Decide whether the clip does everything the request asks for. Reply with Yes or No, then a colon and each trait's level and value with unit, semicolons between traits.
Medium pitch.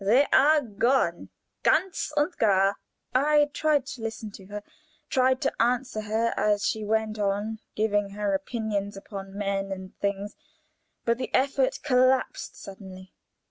No: high, 215 Hz